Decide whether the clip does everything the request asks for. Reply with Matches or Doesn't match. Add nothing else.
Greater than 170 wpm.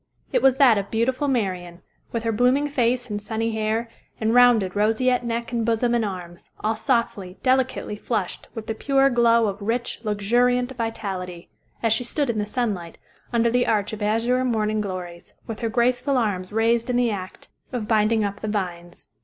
Matches